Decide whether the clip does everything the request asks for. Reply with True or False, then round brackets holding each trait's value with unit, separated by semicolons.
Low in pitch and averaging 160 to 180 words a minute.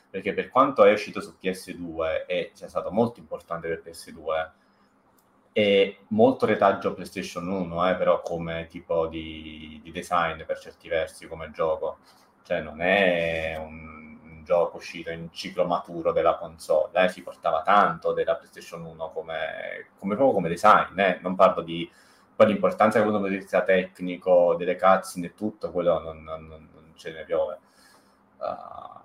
True (85 Hz; 165 wpm)